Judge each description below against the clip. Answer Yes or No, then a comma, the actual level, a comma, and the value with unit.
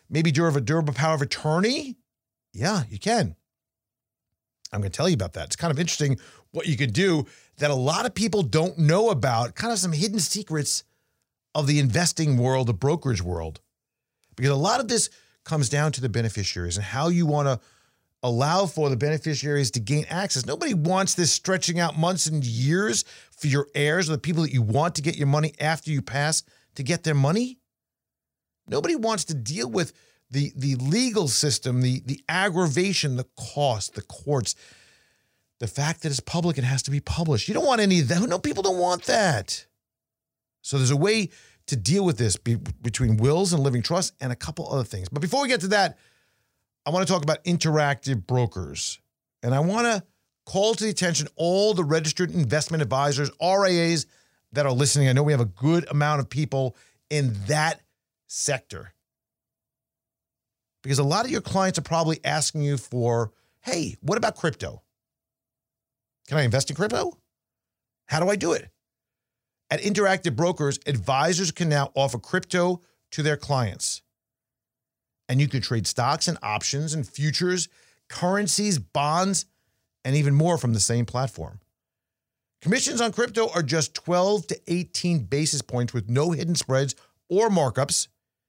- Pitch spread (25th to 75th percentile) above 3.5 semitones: Yes, average, 4.9 semitones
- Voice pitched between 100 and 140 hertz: No, medium, 150 Hz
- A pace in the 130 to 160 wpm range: No, average, 180 wpm